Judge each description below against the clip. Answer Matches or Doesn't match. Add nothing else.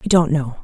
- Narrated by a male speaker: Doesn't match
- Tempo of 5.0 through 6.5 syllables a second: Matches